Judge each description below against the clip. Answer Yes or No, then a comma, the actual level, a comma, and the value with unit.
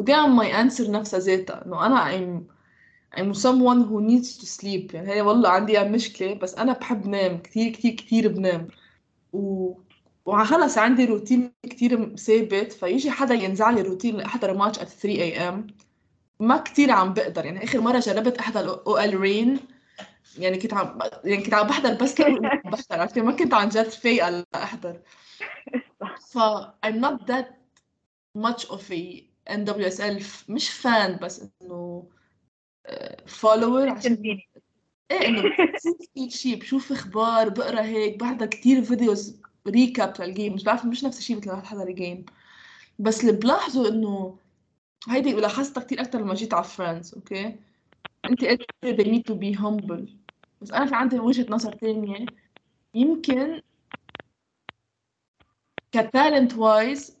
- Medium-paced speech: No, fast, 150 wpm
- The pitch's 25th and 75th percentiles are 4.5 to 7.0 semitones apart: No, average, 3.9 semitones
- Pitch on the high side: Yes, high, 220 Hz